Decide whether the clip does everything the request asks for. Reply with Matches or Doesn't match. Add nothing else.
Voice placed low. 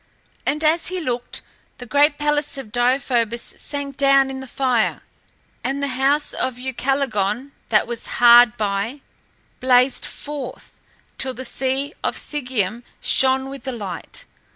Doesn't match